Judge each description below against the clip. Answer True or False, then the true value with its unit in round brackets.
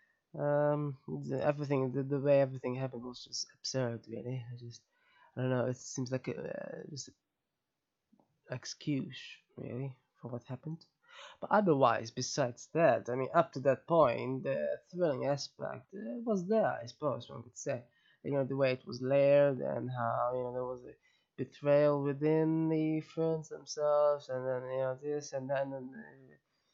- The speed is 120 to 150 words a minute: False (170 wpm)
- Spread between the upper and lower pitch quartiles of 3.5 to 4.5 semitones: False (2.8 semitones)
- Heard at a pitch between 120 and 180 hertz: True (135 Hz)